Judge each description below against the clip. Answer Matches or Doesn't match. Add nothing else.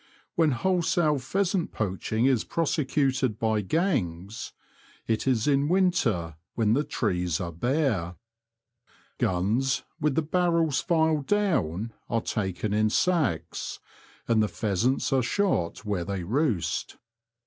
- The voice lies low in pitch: Matches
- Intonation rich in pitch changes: Matches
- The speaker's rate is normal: Doesn't match